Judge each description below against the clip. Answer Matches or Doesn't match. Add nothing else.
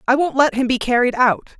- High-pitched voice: Matches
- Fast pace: Matches